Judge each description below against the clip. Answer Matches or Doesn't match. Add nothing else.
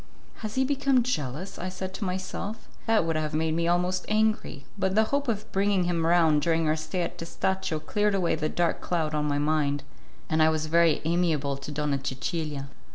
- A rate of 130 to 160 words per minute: Doesn't match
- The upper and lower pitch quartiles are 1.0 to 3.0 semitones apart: Doesn't match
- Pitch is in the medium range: Matches